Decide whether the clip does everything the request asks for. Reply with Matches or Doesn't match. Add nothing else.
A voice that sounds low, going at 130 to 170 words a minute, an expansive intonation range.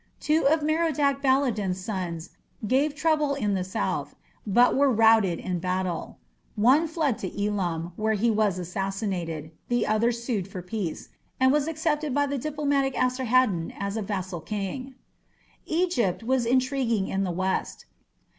Doesn't match